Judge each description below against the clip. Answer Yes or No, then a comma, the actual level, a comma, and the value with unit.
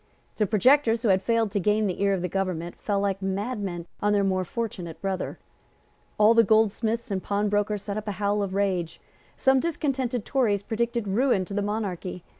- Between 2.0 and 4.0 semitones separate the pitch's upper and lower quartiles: Yes, average, 2.7 semitones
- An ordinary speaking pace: Yes, average, 190 wpm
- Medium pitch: No, high, 205 Hz